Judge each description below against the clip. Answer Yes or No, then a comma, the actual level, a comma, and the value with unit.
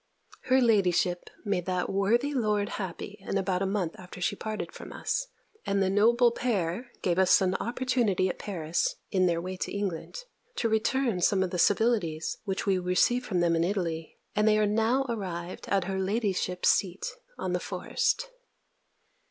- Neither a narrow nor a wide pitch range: Yes, average, 3.6 semitones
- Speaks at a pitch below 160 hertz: No, high, 195 Hz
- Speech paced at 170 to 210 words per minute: Yes, average, 175 wpm